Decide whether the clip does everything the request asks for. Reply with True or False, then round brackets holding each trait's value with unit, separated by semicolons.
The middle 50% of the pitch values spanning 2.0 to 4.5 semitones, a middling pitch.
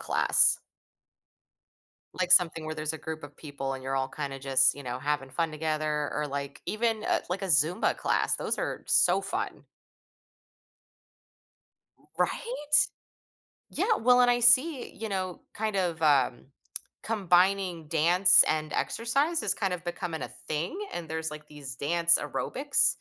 False (5.1 semitones; 165 Hz)